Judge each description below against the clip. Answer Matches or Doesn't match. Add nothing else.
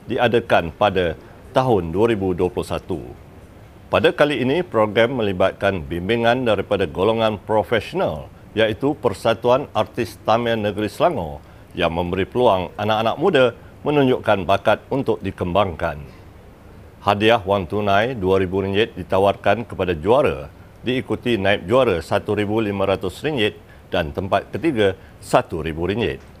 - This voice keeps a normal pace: Matches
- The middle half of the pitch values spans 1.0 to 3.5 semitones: Matches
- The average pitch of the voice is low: Matches